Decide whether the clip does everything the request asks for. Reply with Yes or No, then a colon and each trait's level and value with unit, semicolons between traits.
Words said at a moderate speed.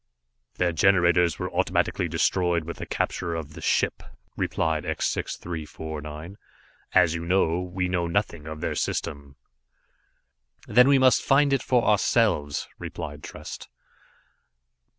No: slow, 130 wpm